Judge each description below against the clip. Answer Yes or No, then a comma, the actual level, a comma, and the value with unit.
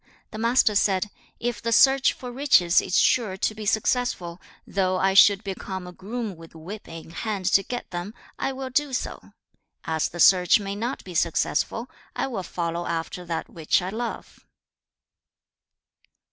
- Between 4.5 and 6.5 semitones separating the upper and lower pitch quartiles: Yes, average, 4.8 semitones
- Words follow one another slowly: No, average, 165 wpm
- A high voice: Yes, high, 195 Hz